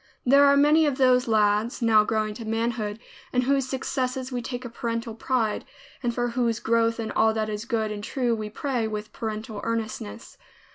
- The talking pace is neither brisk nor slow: Yes, average, 190 wpm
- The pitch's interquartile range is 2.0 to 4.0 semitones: Yes, narrow, 2.6 semitones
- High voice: Yes, high, 230 Hz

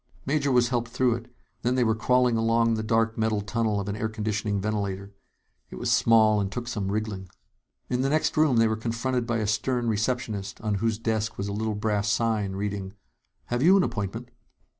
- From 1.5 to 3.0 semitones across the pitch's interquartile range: Yes, narrow, 2.5 semitones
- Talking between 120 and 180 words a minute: No, fast, 205 wpm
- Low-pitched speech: Yes, low, 110 Hz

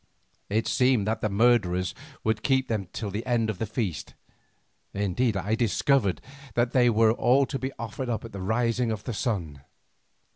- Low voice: Yes, low, 110 Hz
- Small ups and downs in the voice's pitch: No, average, 3.2 semitones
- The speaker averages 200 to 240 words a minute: No, average, 175 wpm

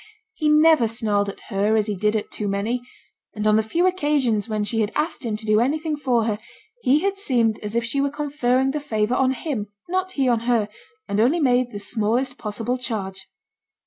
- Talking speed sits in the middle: No, fast, 210 wpm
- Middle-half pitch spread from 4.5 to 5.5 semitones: Yes, average, 4.8 semitones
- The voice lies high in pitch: Yes, high, 235 Hz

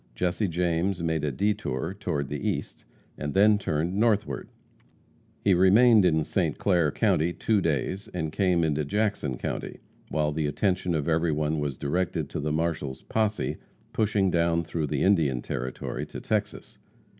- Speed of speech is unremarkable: Yes, average, 155 wpm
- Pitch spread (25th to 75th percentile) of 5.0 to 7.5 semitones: No, average, 4.4 semitones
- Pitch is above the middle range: No, very low, 85 Hz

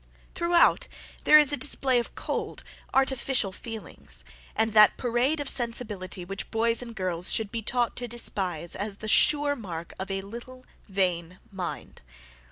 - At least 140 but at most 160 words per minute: Yes, average, 155 wpm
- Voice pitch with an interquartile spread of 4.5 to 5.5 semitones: Yes, average, 4.8 semitones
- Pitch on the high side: Yes, high, 225 Hz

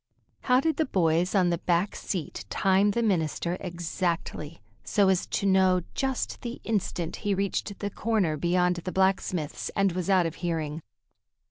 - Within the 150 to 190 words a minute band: Yes, average, 160 wpm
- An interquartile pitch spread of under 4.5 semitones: Yes, average, 2.7 semitones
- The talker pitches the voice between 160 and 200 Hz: Yes, medium, 185 Hz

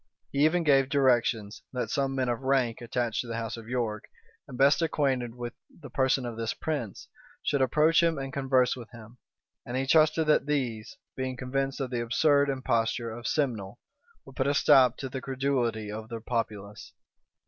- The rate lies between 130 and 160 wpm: No, average, 185 wpm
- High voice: No, low, 130 Hz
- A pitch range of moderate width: Yes, average, 3.0 semitones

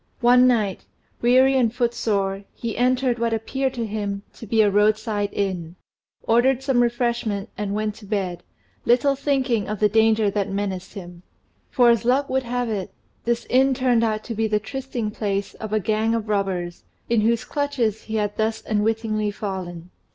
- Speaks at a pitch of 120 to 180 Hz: No, high, 220 Hz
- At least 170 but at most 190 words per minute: Yes, average, 175 wpm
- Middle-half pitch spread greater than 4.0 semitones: No, average, 2.9 semitones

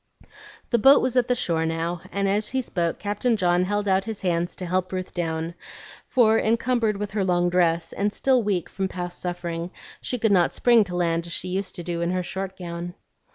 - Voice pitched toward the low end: No, medium, 185 Hz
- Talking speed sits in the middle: No, fast, 215 wpm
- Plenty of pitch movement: No, average, 3.2 semitones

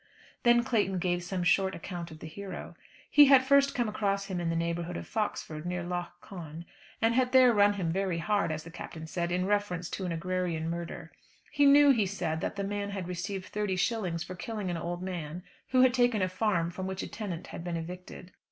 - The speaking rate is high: Yes, fast, 220 wpm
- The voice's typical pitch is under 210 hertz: Yes, medium, 185 Hz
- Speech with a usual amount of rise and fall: Yes, average, 3.3 semitones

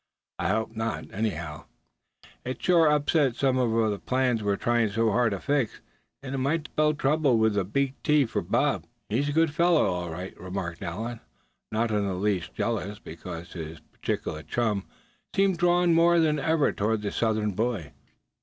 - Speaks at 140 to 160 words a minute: No, average, 175 wpm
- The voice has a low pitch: Yes, low, 115 Hz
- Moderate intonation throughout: No, wide, 6.3 semitones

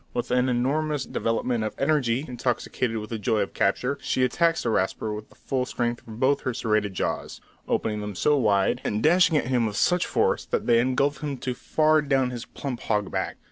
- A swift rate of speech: Yes, fast, 210 wpm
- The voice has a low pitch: Yes, low, 125 Hz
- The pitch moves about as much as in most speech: Yes, average, 4.0 semitones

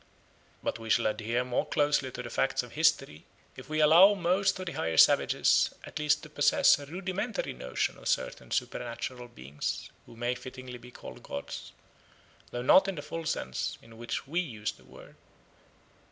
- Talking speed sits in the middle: Yes, average, 180 wpm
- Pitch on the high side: No, low, 130 Hz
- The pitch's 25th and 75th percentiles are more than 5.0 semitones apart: Yes, wide, 5.6 semitones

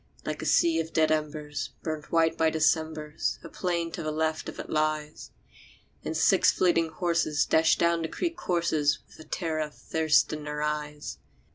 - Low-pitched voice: No, medium, 160 Hz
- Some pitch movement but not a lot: No, narrow, 1.5 semitones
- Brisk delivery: No, average, 180 wpm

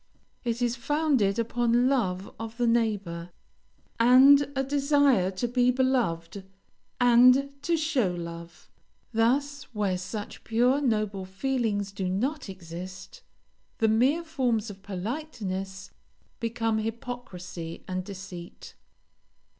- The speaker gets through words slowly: Yes, slow, 110 wpm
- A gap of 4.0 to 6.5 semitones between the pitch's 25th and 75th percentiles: Yes, average, 5.3 semitones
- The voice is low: No, high, 225 Hz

